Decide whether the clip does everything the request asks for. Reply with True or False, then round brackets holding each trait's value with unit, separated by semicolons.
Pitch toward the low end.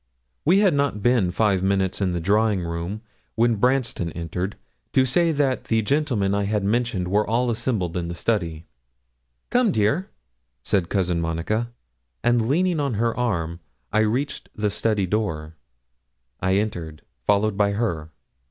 True (105 Hz)